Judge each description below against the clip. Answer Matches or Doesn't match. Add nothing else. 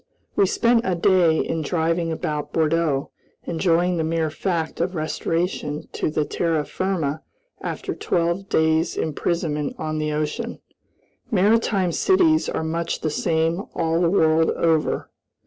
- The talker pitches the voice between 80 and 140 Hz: Doesn't match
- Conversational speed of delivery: Doesn't match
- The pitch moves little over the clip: Matches